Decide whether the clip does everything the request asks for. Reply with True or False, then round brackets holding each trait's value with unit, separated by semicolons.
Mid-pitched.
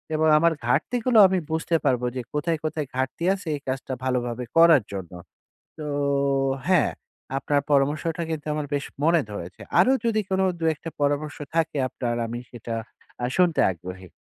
True (145 Hz)